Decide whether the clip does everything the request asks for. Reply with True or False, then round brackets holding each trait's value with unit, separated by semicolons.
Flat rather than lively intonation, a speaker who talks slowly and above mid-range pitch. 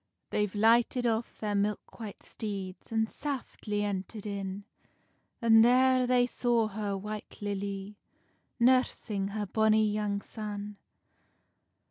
True (2.3 semitones; 115 wpm; 210 Hz)